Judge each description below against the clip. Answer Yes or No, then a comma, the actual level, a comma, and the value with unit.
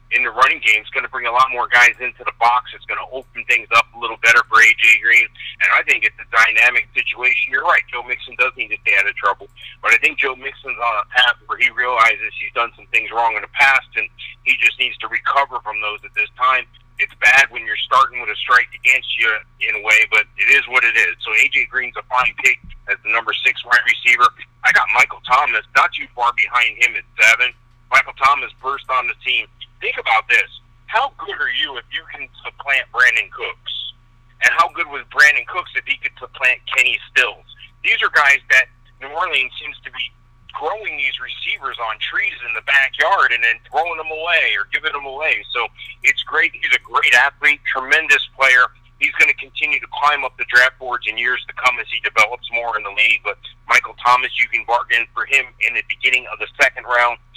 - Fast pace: Yes, fast, 230 wpm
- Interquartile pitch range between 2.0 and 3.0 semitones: No, average, 3.9 semitones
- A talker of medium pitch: No, low, 125 Hz